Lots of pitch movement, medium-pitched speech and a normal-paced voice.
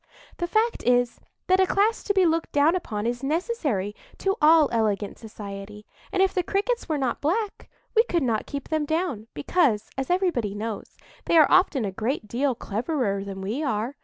No: wide, 8.7 semitones; very high, 280 Hz; average, 190 wpm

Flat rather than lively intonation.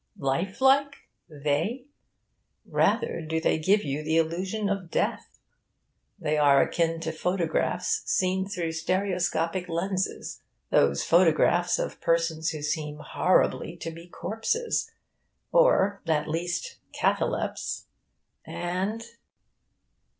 No: average, 3.2 semitones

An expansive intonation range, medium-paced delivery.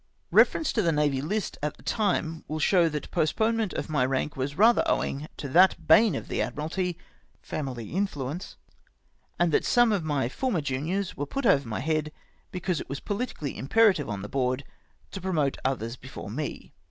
Yes: wide, 5.8 semitones; average, 190 wpm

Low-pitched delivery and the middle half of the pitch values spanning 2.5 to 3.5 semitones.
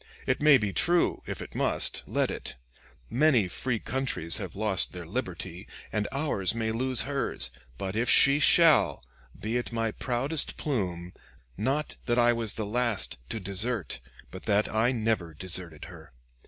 No: low, 110 Hz; wide, 5.4 semitones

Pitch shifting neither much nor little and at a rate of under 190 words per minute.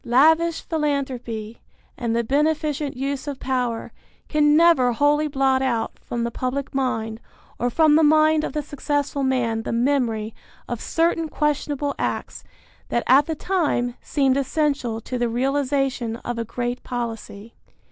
Yes: average, 3.7 semitones; average, 145 wpm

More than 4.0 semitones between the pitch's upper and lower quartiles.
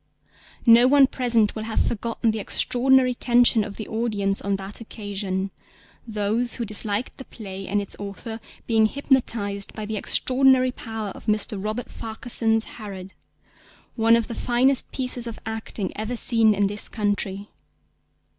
No: average, 2.8 semitones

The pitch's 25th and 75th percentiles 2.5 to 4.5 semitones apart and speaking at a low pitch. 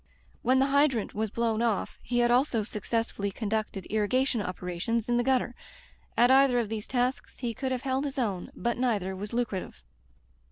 No: average, 3.3 semitones; high, 235 Hz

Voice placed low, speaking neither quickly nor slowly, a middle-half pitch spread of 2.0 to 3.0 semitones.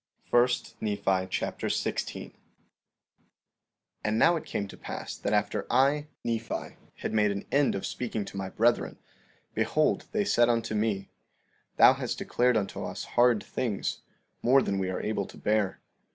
No: low, 110 Hz; average, 160 wpm; average, 3.5 semitones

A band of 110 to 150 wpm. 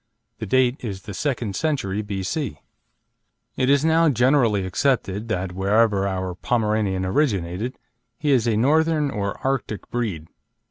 Yes: slow, 135 wpm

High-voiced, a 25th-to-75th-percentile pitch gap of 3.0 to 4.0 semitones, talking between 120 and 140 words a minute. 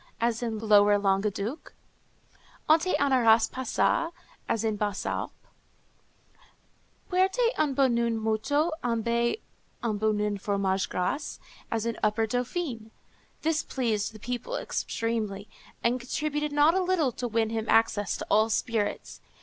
No: high, 230 Hz; average, 4.6 semitones; slow, 135 wpm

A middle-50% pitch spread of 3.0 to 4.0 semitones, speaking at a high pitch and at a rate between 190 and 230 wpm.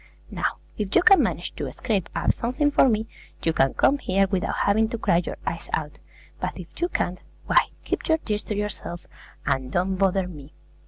No: average, 4.9 semitones; high, 195 Hz; average, 200 wpm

